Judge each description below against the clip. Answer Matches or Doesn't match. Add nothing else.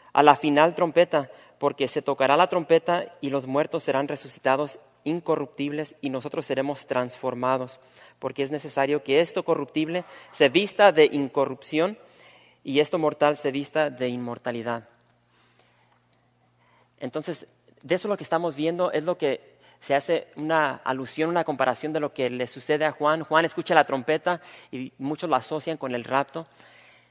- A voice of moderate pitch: Matches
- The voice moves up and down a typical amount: Matches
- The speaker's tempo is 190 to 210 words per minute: Doesn't match